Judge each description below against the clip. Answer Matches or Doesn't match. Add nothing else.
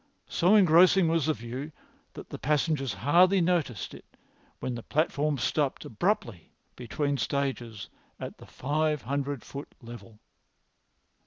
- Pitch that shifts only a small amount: Doesn't match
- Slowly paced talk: Matches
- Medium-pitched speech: Matches